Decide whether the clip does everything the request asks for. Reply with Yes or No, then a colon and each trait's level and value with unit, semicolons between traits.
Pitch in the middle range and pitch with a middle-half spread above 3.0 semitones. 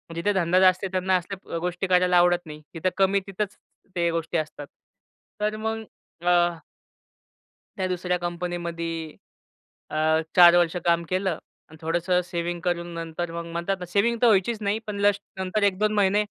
No: medium, 180 Hz; narrow, 2.4 semitones